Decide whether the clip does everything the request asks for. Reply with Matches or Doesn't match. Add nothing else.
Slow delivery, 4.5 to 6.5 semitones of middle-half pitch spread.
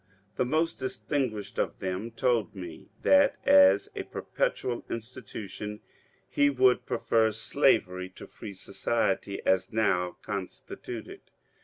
Matches